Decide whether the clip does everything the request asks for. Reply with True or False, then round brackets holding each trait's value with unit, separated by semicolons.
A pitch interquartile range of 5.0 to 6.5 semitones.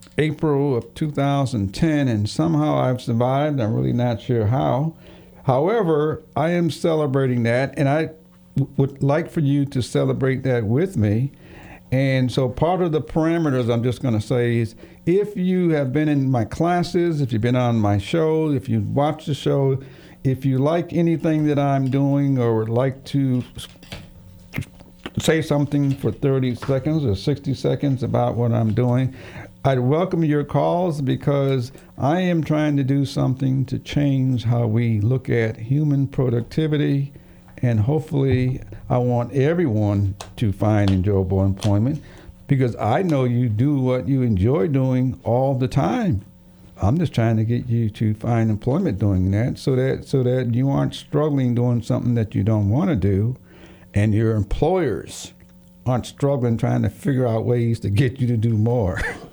False (4.0 semitones)